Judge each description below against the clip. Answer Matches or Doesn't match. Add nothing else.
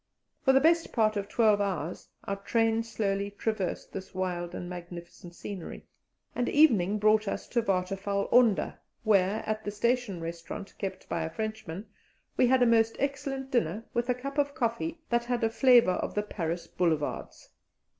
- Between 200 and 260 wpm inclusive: Doesn't match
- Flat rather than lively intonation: Doesn't match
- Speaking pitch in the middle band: Doesn't match